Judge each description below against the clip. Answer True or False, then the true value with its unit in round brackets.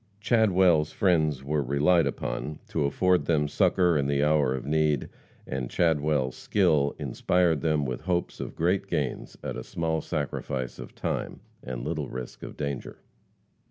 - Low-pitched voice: True (75 Hz)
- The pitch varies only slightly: False (3.3 semitones)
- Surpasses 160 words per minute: False (155 wpm)